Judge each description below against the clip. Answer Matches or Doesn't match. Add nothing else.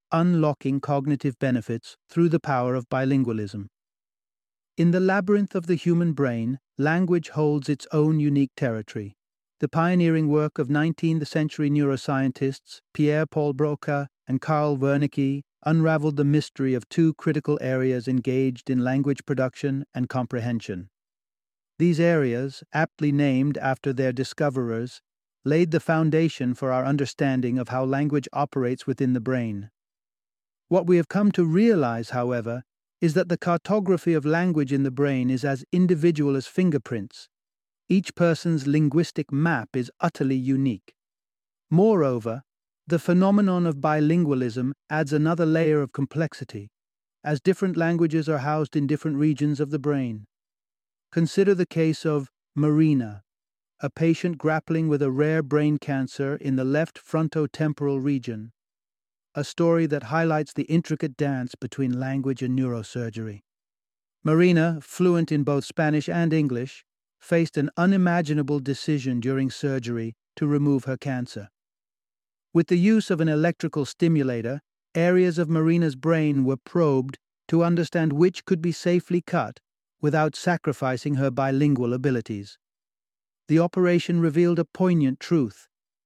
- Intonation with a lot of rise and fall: Doesn't match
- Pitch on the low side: Doesn't match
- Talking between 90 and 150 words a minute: Matches